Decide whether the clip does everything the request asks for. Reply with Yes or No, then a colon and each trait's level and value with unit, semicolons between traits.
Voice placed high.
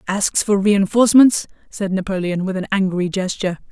Yes: high, 195 Hz